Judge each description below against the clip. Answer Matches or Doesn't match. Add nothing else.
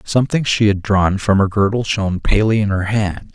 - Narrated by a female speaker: Doesn't match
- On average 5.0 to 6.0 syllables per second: Matches